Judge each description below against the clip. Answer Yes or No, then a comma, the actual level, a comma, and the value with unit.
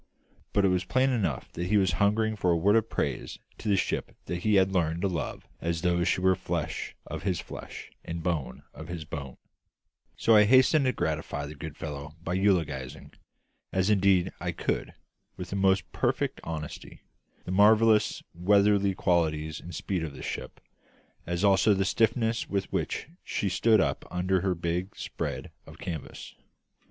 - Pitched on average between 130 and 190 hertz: No, very low, 95 Hz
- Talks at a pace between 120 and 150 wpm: No, average, 175 wpm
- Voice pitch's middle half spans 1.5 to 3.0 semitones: No, average, 3.4 semitones